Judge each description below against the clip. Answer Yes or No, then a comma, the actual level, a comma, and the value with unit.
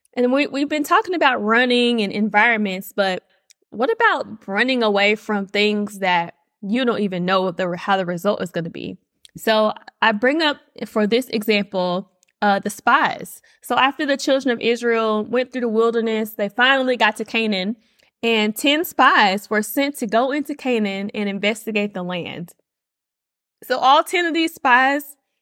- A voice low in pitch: No, high, 225 Hz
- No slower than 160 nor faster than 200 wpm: Yes, average, 170 wpm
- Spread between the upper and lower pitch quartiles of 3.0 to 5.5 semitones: Yes, average, 4.1 semitones